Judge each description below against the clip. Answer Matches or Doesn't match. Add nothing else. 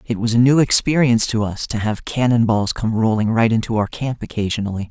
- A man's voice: Matches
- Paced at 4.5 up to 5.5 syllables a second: Doesn't match